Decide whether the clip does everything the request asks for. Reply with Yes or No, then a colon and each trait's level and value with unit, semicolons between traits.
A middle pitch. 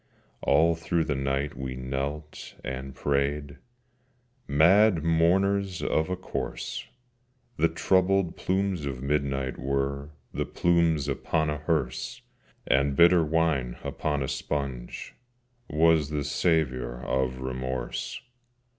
No: very low, 75 Hz